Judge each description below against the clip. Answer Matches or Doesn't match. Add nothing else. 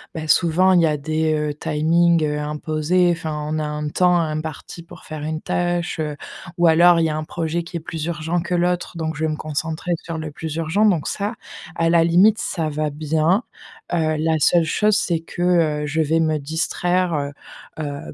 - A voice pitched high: Doesn't match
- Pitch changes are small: Matches